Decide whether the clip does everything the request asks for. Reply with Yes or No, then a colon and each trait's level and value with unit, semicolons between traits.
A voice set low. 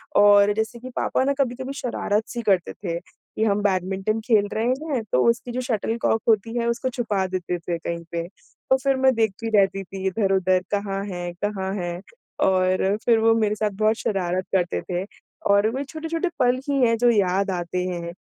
No: high, 205 Hz